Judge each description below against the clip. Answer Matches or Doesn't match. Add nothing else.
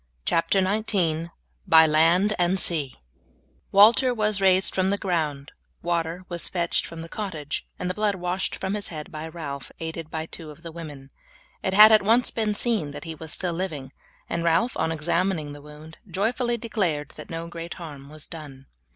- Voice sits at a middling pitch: Matches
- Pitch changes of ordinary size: Matches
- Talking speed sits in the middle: Matches